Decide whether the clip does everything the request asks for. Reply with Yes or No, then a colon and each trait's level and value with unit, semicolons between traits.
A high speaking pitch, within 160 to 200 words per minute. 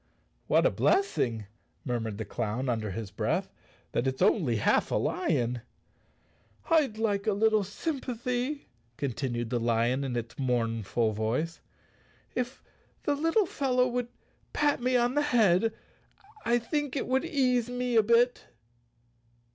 No: high, 215 Hz; average, 140 wpm